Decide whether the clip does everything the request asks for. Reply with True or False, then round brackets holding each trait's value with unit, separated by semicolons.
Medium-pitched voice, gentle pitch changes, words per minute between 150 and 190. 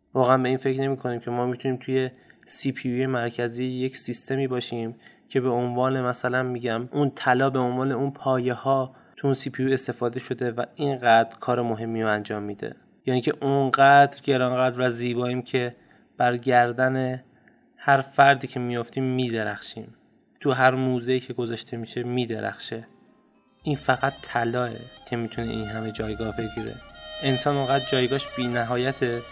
False (125 Hz; 1.8 semitones; 155 wpm)